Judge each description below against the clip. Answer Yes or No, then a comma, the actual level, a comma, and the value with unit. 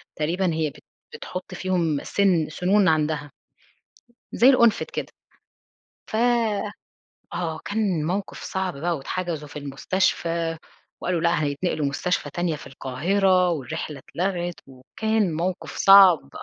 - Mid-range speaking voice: Yes, medium, 170 Hz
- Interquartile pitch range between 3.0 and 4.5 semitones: Yes, average, 3.7 semitones